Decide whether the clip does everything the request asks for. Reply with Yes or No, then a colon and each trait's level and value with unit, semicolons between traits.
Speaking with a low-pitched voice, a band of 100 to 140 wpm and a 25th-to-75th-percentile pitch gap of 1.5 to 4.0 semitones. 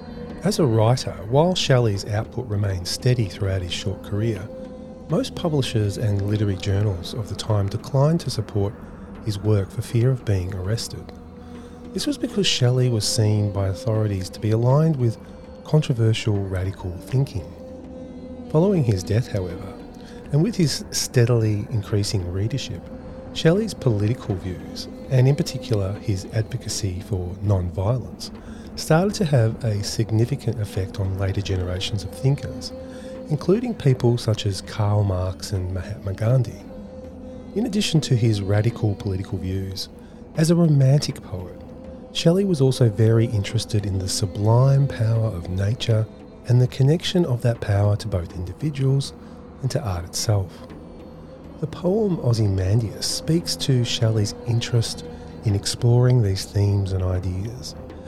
No: low, 110 Hz; slow, 135 wpm; average, 4.8 semitones